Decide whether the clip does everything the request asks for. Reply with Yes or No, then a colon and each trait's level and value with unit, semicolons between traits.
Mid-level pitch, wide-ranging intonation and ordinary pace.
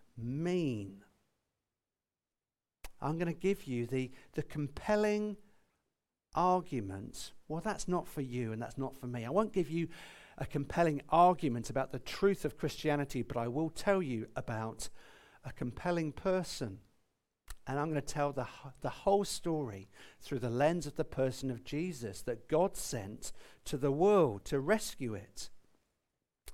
Yes: medium, 145 Hz; wide, 5.8 semitones; average, 150 wpm